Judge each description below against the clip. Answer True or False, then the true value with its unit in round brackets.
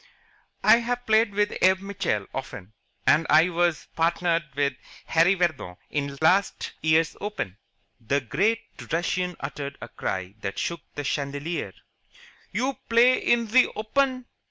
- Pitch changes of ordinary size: False (6.8 semitones)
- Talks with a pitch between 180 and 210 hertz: False (170 Hz)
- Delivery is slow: True (130 wpm)